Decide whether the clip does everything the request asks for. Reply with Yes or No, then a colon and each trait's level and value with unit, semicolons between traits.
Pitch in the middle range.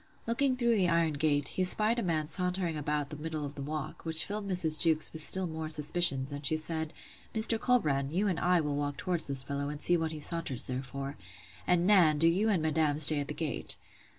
Yes: medium, 160 Hz